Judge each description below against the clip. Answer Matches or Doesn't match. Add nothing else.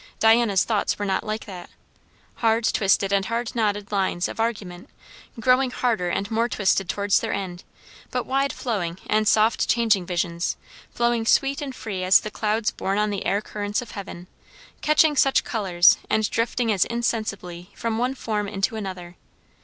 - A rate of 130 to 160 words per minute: Doesn't match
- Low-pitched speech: Doesn't match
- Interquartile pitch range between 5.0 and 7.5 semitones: Doesn't match